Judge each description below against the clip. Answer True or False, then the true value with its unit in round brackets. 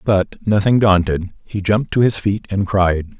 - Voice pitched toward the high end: False (100 Hz)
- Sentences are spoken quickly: False (190 wpm)